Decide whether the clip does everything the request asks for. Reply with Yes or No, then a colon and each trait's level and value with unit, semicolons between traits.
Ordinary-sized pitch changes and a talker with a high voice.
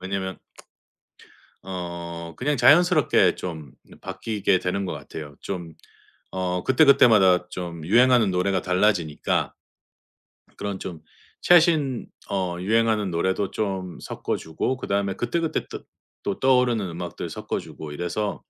No: average, 4.5 semitones; very low, 95 Hz